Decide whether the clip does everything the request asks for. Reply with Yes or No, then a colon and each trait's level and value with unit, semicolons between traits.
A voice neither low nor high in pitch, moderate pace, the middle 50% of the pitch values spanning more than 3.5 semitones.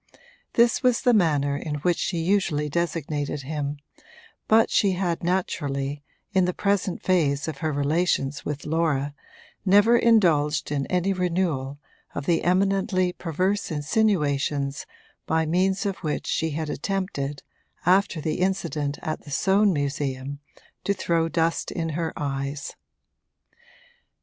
No: medium, 165 Hz; slow, 130 wpm; average, 4.4 semitones